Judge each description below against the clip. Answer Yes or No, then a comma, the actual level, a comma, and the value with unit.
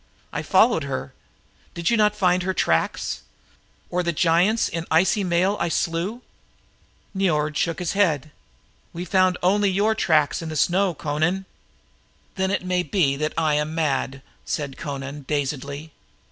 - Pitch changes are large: No, average, 4.0 semitones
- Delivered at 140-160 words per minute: Yes, average, 145 wpm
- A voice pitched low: No, medium, 170 Hz